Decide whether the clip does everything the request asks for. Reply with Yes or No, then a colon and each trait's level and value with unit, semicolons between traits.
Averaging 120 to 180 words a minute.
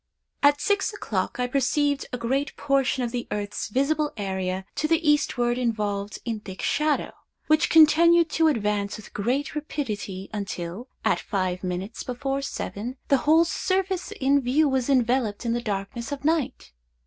Yes: average, 160 wpm